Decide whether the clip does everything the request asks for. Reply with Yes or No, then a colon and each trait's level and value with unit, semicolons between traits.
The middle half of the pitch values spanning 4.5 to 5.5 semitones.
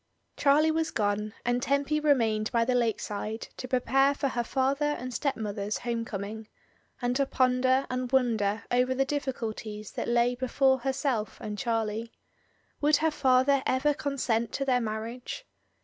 No: average, 3.4 semitones